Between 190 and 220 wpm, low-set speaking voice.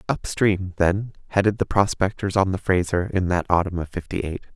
Yes: average, 200 wpm; very low, 95 Hz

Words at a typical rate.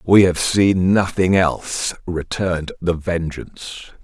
No: slow, 120 wpm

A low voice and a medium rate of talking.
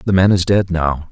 No: very low, 90 Hz; fast, 270 wpm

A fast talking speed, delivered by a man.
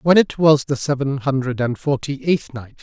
Yes: fast, 210 wpm; male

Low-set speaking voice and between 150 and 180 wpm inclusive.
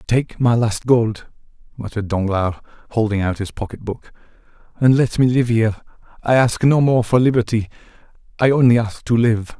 Yes: low, 115 Hz; average, 165 wpm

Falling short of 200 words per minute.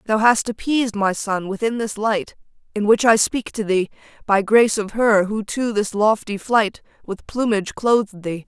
Yes: average, 190 wpm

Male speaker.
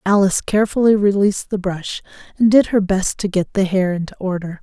No: female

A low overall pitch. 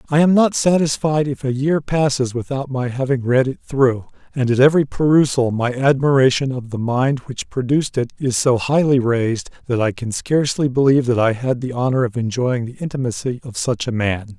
Yes: low, 130 Hz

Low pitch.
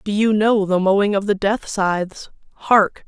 No: high, 200 Hz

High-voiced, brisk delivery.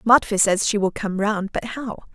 Yes: high, 210 Hz; fast, 225 wpm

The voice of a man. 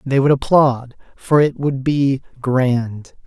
Yes: male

